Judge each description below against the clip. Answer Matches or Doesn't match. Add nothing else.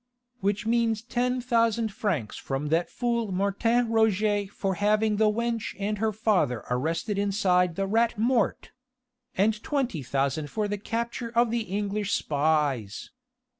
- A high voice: Matches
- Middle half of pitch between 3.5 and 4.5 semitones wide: Matches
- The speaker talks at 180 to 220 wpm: Doesn't match